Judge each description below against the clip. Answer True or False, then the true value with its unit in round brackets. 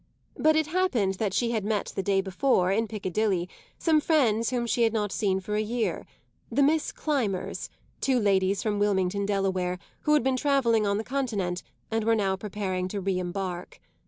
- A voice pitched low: False (210 Hz)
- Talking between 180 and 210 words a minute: True (190 wpm)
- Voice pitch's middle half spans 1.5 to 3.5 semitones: False (3.9 semitones)